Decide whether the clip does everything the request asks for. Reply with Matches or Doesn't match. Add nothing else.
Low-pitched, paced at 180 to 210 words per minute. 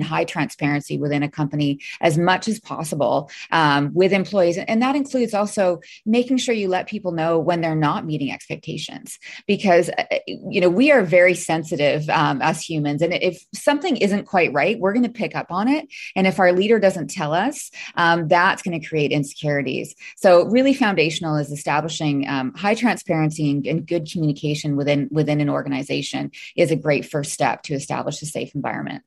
Doesn't match